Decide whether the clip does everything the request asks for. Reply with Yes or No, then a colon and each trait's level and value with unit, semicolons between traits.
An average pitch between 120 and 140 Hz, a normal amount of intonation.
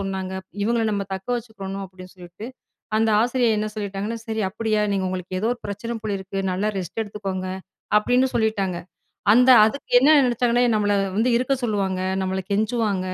No: high, 210 Hz; average, 3.1 semitones